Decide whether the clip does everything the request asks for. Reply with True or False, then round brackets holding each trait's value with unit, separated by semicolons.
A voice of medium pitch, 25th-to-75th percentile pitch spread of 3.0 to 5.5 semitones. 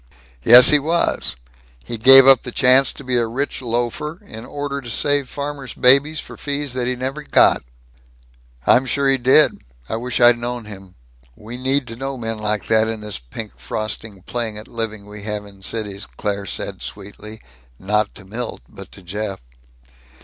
False (120 Hz; 4.0 semitones)